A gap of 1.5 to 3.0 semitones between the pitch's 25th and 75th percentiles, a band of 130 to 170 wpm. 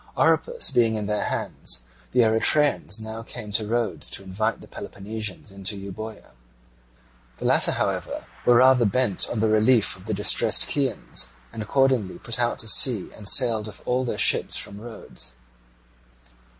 Yes: average, 2.7 semitones; average, 160 wpm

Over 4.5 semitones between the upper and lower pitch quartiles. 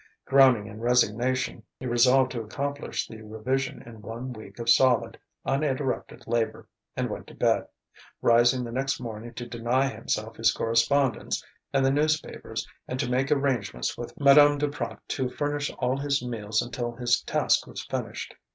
No: narrow, 2.5 semitones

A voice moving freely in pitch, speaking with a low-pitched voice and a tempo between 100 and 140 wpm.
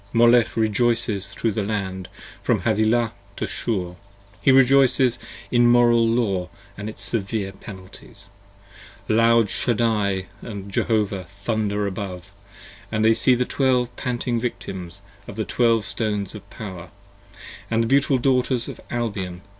No: average, 3.2 semitones; low, 110 Hz; slow, 135 wpm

